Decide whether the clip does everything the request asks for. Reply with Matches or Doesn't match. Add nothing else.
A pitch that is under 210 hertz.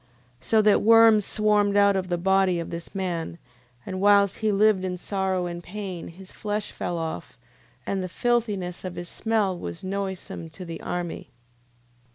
Matches